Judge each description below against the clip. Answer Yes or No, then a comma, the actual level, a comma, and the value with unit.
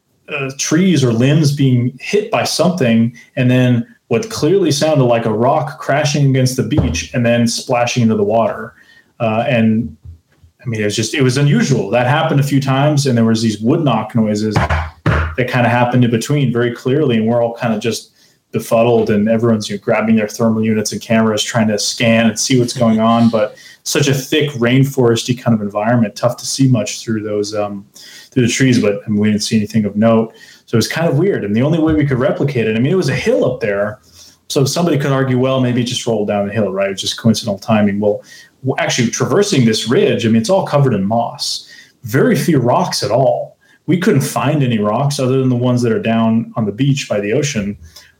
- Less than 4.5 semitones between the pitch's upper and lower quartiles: Yes, average, 3.3 semitones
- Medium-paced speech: No, fast, 225 wpm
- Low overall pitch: Yes, low, 120 Hz